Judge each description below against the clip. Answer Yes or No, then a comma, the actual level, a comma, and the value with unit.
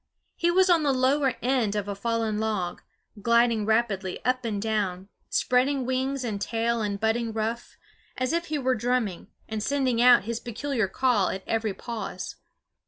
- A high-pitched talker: Yes, high, 235 Hz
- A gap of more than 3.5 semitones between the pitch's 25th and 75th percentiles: No, average, 3.2 semitones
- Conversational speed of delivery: Yes, average, 170 wpm